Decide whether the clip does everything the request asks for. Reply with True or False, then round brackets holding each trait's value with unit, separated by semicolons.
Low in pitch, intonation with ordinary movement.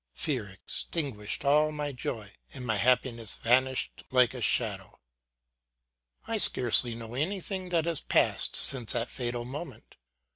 True (125 Hz; 4.1 semitones)